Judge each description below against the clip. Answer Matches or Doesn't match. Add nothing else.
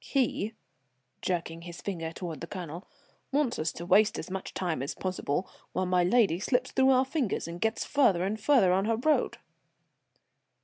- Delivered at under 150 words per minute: Doesn't match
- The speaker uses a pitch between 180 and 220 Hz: Matches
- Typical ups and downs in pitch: Doesn't match